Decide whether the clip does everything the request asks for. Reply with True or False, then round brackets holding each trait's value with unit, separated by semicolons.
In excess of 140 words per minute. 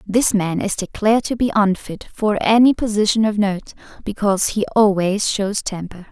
True (165 wpm)